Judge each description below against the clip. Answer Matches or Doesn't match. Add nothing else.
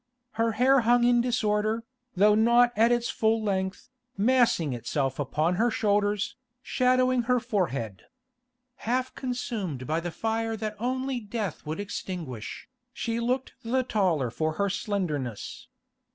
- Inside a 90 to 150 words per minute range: Matches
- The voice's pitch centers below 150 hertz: Doesn't match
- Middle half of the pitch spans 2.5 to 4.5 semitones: Doesn't match